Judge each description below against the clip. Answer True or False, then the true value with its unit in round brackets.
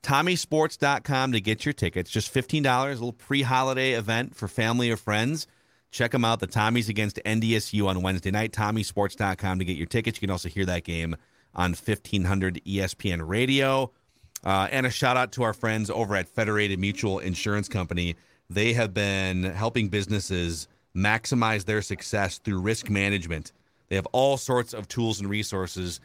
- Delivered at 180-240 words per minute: False (170 wpm)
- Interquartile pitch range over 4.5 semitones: False (3.8 semitones)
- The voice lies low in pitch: True (105 Hz)